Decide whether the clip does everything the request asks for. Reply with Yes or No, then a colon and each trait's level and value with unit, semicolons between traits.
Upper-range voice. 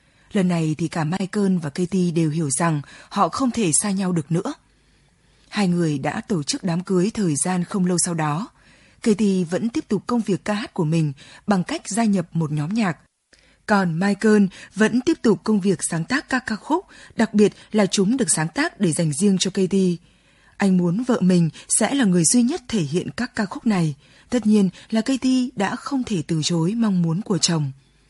Yes: high, 195 Hz